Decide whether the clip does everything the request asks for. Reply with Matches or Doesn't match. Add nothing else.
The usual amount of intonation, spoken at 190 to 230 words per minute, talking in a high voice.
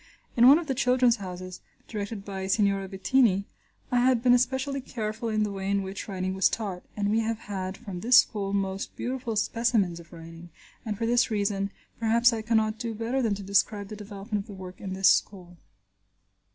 Matches